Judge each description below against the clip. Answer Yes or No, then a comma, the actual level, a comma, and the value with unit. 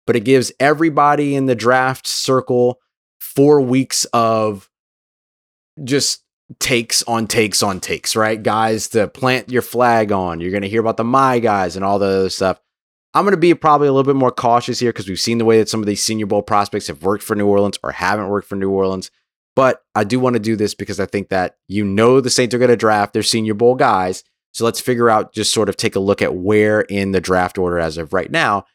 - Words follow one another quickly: Yes, fast, 240 wpm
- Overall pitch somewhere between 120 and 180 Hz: No, low, 110 Hz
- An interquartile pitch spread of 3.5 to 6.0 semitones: Yes, average, 3.9 semitones